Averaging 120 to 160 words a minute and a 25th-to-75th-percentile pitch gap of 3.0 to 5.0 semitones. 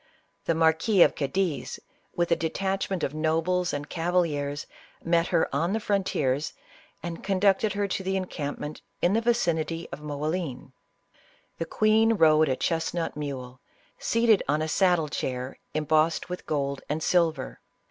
Yes: average, 150 wpm; average, 3.8 semitones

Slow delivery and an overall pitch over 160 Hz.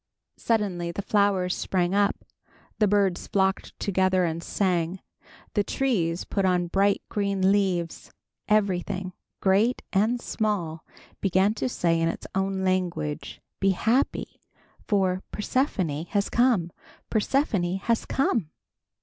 Yes: slow, 120 wpm; high, 190 Hz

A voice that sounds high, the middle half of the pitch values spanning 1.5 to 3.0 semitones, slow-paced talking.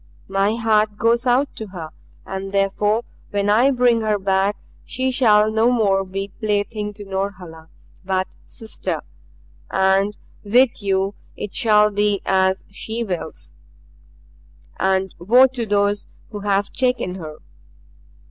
Yes: high, 205 Hz; narrow, 2.6 semitones; slow, 130 wpm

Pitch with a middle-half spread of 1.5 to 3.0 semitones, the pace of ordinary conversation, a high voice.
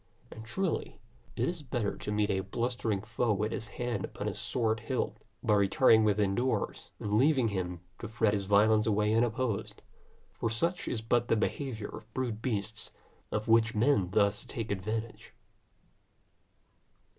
No: narrow, 2.5 semitones; average, 155 wpm; low, 110 Hz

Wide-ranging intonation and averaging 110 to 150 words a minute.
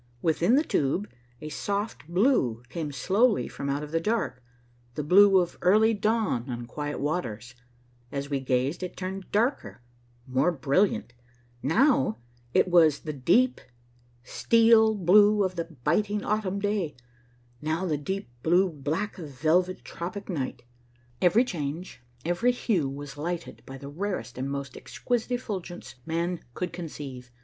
Yes: wide, 6.2 semitones; average, 140 wpm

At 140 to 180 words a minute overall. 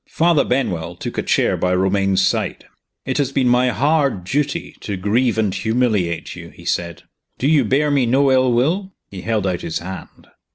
No: average, 190 wpm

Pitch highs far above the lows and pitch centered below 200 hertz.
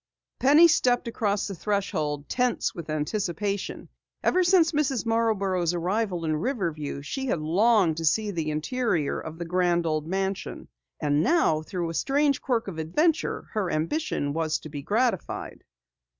Yes: wide, 7.0 semitones; high, 190 Hz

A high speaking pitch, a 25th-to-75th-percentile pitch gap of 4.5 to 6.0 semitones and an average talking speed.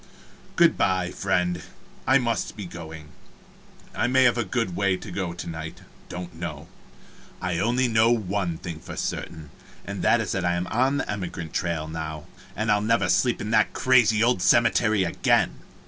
No: very low, 95 Hz; average, 5.1 semitones; average, 180 wpm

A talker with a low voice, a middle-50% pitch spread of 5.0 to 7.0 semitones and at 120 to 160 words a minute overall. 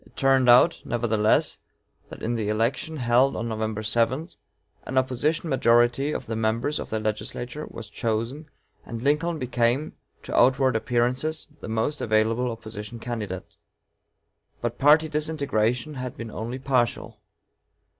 No: low, 120 Hz; average, 3.5 semitones; slow, 135 wpm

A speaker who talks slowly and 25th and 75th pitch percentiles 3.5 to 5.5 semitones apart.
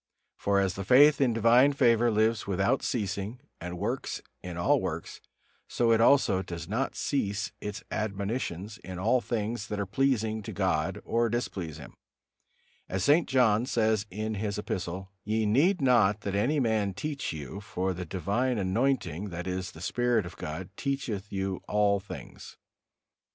No: average, 165 wpm; average, 3.9 semitones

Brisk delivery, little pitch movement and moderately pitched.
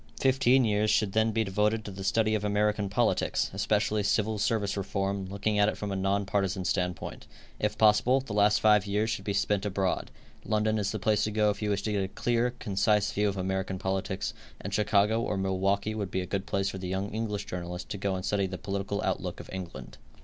No: fast, 220 wpm; narrow, 1.8 semitones; low, 100 Hz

